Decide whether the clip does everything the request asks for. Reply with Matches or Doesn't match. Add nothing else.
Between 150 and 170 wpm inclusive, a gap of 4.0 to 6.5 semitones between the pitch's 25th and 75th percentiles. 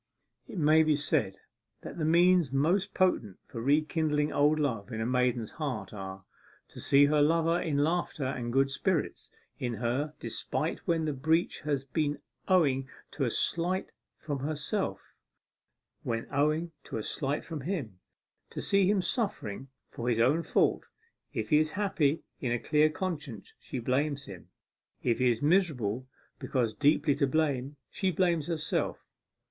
Matches